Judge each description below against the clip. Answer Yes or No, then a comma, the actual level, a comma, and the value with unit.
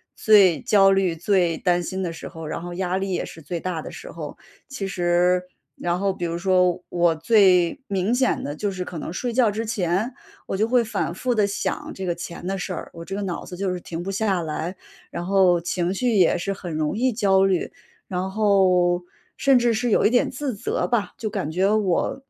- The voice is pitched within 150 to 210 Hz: Yes, high, 190 Hz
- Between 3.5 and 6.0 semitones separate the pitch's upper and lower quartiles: No, average, 3.1 semitones